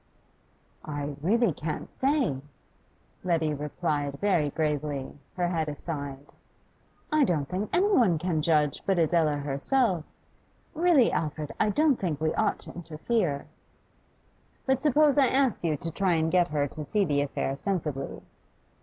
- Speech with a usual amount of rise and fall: No, wide, 6.1 semitones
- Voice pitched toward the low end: No, medium, 165 Hz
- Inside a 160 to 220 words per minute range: No, average, 145 wpm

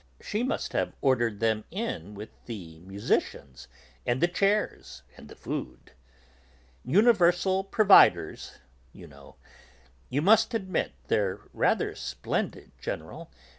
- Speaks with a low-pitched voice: Yes, low, 130 Hz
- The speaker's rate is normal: No, slow, 115 wpm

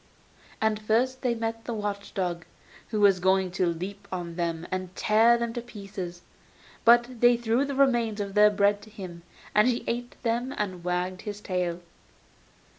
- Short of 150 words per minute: No, average, 175 wpm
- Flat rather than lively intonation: No, average, 4.1 semitones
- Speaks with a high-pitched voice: Yes, high, 210 Hz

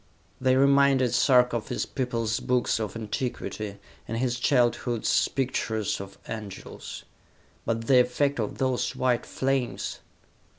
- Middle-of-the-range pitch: No, low, 125 Hz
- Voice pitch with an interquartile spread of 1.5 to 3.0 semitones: Yes, narrow, 2.4 semitones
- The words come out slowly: Yes, slow, 125 wpm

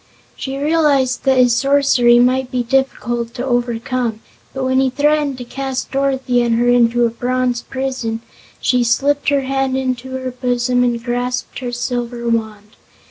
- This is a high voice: Yes, very high, 250 Hz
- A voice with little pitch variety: Yes, narrow, 1.8 semitones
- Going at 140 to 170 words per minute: Yes, average, 160 wpm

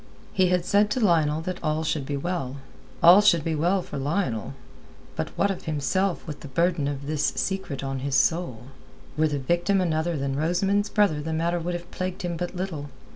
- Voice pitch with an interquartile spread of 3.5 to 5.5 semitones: Yes, average, 3.9 semitones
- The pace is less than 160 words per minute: No, average, 200 wpm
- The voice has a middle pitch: Yes, medium, 165 Hz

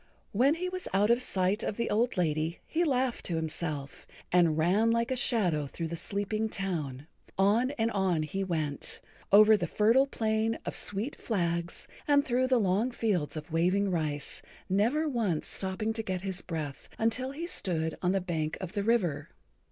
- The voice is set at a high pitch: Yes, high, 195 Hz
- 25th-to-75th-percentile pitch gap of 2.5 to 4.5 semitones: No, wide, 5.4 semitones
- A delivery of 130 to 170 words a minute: No, average, 180 wpm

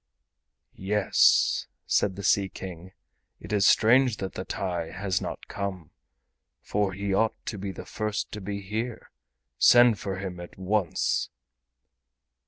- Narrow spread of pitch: Yes, narrow, 2.0 semitones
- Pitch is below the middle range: Yes, low, 100 Hz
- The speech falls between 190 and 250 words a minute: No, average, 140 wpm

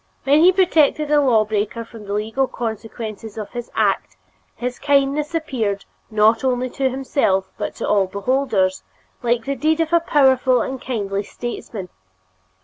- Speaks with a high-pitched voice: Yes, high, 245 Hz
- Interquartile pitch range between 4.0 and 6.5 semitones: Yes, average, 4.6 semitones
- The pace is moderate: Yes, average, 155 wpm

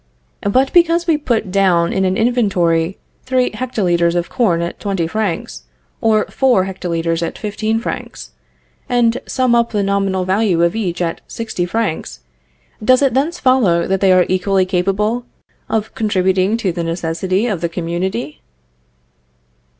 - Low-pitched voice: No, high, 195 Hz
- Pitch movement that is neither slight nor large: Yes, average, 4.7 semitones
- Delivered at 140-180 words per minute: Yes, average, 150 wpm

